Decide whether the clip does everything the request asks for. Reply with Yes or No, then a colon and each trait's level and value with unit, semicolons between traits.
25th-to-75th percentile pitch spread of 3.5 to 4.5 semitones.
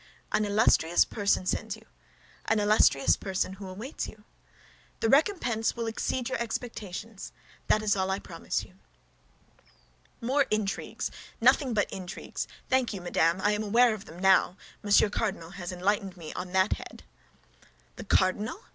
No: average, 3.0 semitones